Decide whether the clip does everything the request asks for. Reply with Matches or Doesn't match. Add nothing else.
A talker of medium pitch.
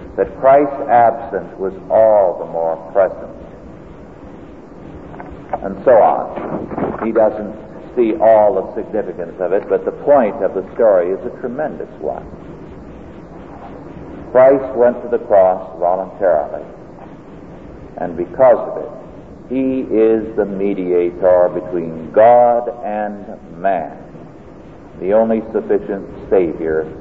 Doesn't match